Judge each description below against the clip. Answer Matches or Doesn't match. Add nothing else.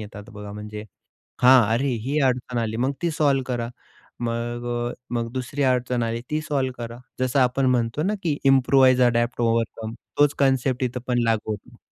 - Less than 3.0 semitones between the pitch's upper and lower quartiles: Matches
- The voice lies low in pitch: Matches